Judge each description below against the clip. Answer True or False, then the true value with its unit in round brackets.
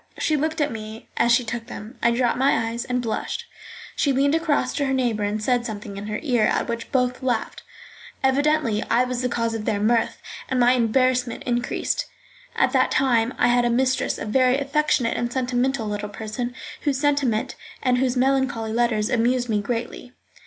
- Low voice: False (245 Hz)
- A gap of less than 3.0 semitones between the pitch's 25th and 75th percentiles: True (2.6 semitones)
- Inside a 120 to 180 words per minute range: False (190 wpm)